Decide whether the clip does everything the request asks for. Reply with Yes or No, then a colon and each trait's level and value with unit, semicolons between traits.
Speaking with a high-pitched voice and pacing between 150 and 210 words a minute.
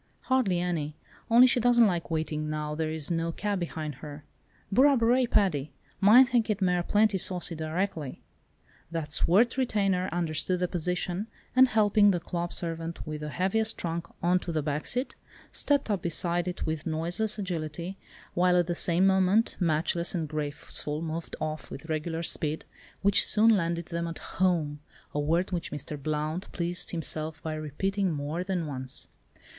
No: medium, 170 Hz; average, 160 wpm